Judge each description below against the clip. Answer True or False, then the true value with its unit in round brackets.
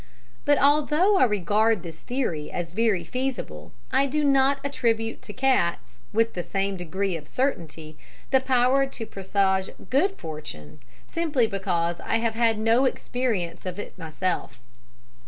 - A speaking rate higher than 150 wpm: False (145 wpm)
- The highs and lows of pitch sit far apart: True (7.0 semitones)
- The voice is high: True (220 Hz)